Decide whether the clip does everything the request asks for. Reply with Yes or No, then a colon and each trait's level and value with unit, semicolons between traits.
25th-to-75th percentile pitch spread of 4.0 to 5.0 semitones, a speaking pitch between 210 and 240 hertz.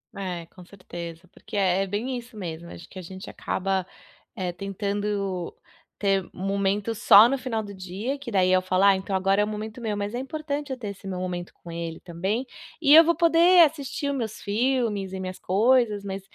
No: average, 4.3 semitones; high, 200 Hz